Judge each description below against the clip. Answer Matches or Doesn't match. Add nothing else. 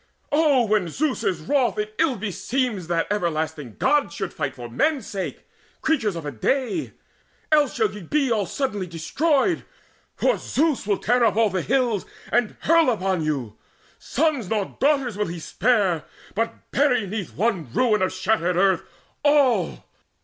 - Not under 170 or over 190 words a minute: Doesn't match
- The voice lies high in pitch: Matches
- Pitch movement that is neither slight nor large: Doesn't match